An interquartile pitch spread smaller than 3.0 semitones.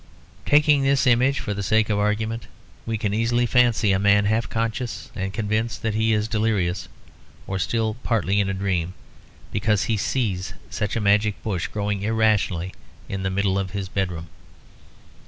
Yes: narrow, 2.5 semitones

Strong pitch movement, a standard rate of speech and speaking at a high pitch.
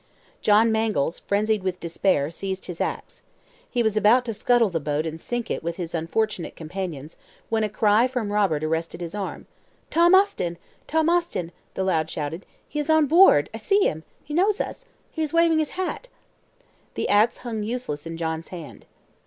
Yes: wide, 7.1 semitones; average, 185 wpm; high, 205 Hz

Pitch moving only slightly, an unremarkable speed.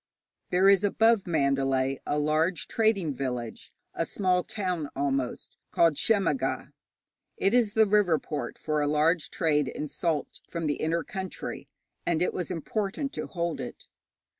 No: average, 4.7 semitones; average, 150 wpm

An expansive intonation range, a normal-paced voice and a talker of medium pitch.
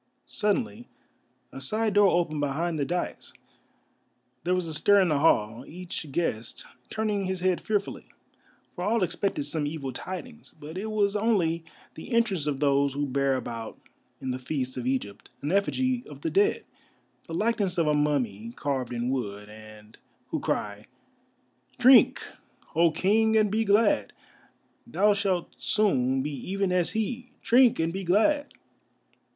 Yes: wide, 7.2 semitones; average, 155 wpm; medium, 175 Hz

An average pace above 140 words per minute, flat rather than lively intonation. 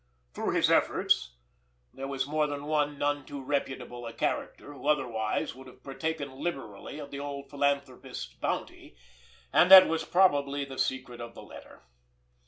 Yes: average, 160 wpm; narrow, 1.8 semitones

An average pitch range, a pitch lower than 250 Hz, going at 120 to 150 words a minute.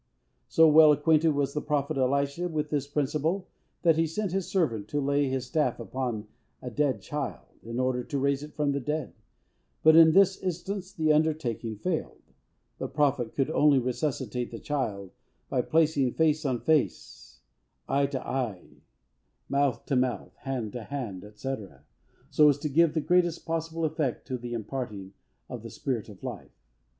No: average, 3.7 semitones; medium, 140 Hz; average, 170 wpm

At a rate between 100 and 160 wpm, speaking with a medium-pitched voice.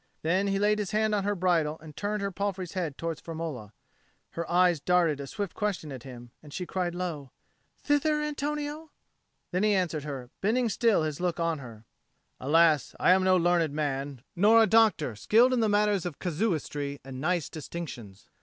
No: average, 180 wpm; medium, 175 Hz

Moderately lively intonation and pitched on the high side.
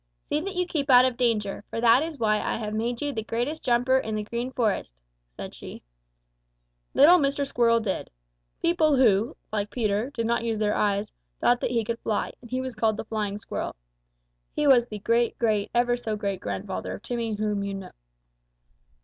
Yes: average, 3.3 semitones; high, 230 Hz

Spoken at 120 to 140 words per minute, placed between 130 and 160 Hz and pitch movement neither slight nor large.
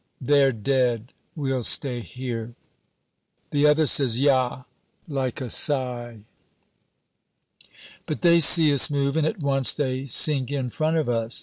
Yes: slow, 135 wpm; low, 135 Hz; average, 3.0 semitones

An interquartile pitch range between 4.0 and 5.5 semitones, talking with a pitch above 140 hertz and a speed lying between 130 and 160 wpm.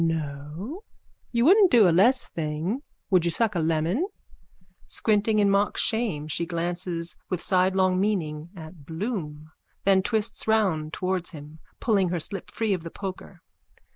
Yes: average, 4.4 semitones; medium, 185 Hz; average, 155 wpm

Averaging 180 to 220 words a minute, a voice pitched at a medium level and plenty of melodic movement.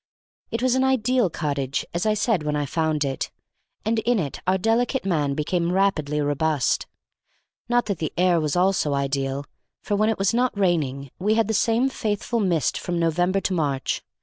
Yes: average, 185 wpm; medium, 180 Hz; wide, 6.5 semitones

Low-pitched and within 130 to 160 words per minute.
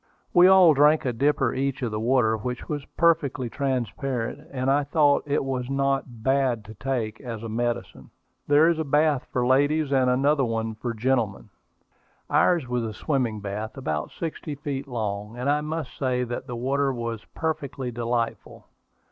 No: low, 130 Hz; average, 170 wpm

